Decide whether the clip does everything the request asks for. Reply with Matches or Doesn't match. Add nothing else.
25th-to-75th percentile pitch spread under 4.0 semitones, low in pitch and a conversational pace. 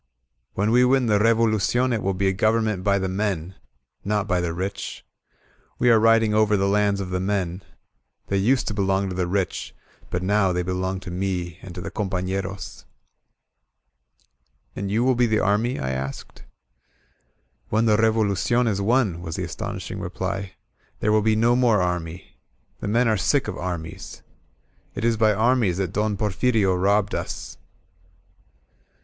Matches